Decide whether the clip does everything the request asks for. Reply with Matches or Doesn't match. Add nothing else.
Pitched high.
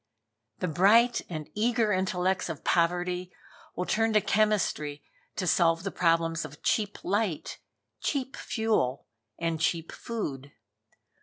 Doesn't match